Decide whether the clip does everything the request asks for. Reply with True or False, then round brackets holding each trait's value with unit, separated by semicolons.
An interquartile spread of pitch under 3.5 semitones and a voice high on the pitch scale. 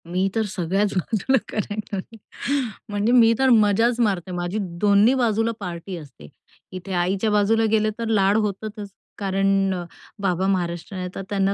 True (2.7 semitones; 200 Hz)